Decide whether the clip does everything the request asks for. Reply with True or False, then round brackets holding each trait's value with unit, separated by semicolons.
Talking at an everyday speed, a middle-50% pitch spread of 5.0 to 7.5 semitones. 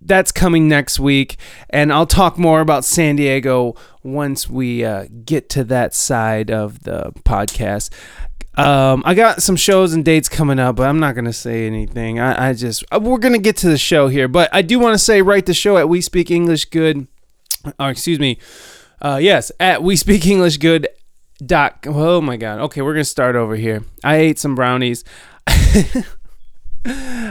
True (190 wpm; 5.6 semitones)